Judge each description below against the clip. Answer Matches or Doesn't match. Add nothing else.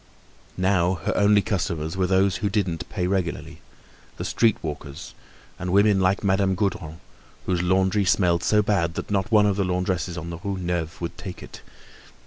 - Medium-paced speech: Matches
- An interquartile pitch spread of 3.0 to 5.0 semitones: Doesn't match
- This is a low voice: Matches